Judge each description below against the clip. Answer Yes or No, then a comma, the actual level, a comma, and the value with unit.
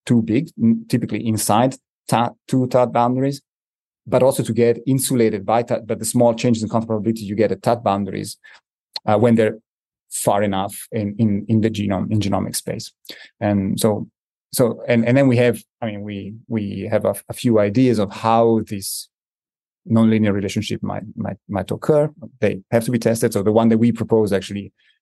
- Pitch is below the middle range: Yes, low, 115 Hz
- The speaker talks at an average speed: Yes, average, 185 wpm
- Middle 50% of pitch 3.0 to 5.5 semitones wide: No, narrow, 2.4 semitones